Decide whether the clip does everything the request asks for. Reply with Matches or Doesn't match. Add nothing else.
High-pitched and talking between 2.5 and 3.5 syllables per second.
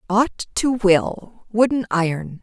Matches